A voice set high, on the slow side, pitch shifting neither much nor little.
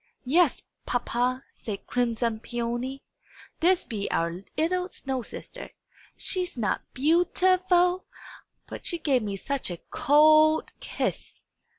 No: very high, 270 Hz; slow, 125 wpm; wide, 6.3 semitones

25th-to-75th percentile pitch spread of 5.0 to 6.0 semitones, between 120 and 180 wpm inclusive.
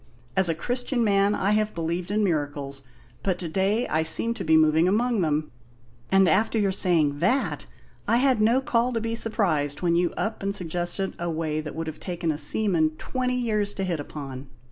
No: wide, 5.4 semitones; average, 200 wpm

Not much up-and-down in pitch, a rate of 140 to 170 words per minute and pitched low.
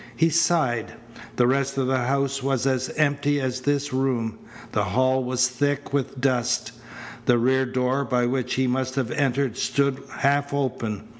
Yes: narrow, 1.8 semitones; average, 165 wpm; low, 130 Hz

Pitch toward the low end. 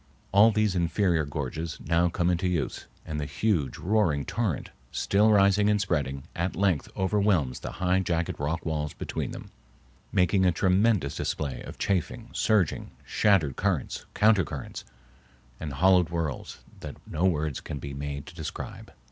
Yes: very low, 85 Hz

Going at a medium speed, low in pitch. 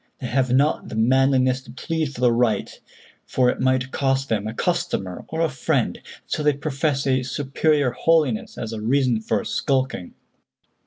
Yes: average, 175 wpm; low, 130 Hz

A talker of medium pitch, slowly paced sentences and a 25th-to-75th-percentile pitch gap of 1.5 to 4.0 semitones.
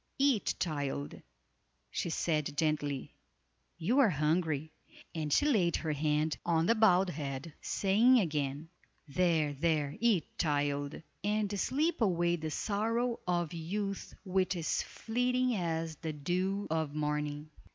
No: medium, 165 Hz; slow, 130 wpm; average, 5.1 semitones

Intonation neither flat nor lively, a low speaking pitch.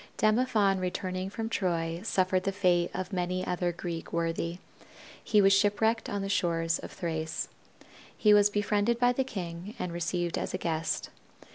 No: average, 3.2 semitones; medium, 185 Hz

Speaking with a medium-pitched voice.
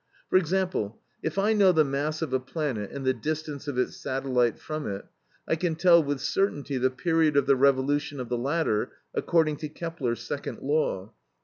Yes: medium, 145 Hz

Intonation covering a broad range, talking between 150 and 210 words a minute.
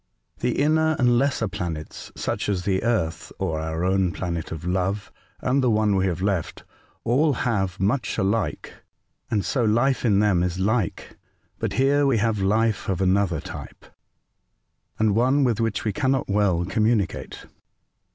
No: average, 4.6 semitones; average, 160 wpm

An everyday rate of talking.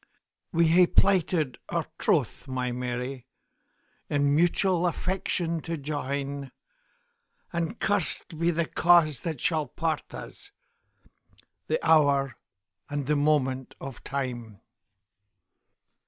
No: slow, 95 wpm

